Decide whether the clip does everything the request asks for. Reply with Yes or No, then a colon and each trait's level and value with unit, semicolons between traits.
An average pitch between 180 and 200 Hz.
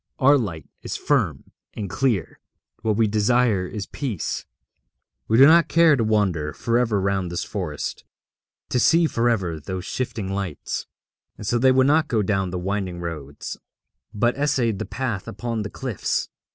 No: low, 110 Hz